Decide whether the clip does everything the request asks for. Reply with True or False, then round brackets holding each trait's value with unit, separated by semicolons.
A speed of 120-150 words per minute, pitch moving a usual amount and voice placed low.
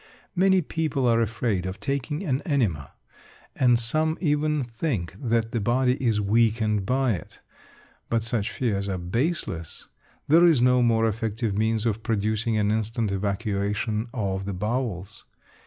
True (145 wpm; 3.8 semitones; 115 Hz)